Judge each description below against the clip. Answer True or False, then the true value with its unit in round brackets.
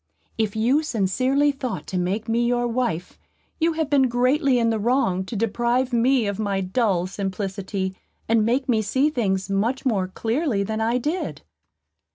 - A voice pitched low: False (230 Hz)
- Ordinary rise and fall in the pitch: True (4.6 semitones)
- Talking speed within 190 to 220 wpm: False (170 wpm)